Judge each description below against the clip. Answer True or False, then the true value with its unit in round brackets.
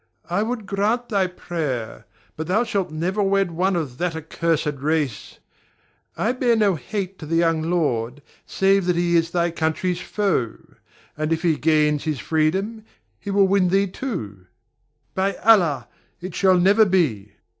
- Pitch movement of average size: True (4.1 semitones)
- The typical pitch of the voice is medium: True (175 Hz)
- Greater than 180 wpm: False (160 wpm)